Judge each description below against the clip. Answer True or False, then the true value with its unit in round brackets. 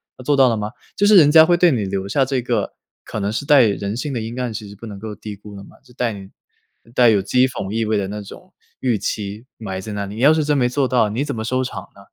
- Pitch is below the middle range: True (115 Hz)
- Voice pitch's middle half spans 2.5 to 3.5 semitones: False (4.2 semitones)